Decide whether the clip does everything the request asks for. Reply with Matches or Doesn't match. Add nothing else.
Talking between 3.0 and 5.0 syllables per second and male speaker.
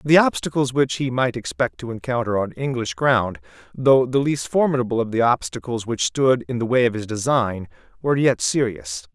Doesn't match